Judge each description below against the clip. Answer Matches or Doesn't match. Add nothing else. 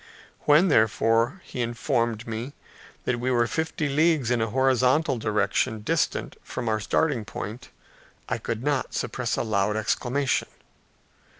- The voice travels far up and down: Doesn't match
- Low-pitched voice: Matches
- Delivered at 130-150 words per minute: Matches